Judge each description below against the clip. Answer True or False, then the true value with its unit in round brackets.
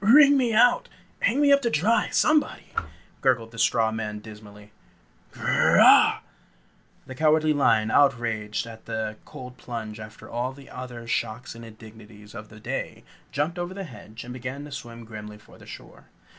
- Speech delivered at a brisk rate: False (170 wpm)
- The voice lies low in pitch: True (120 Hz)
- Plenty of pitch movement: True (5.7 semitones)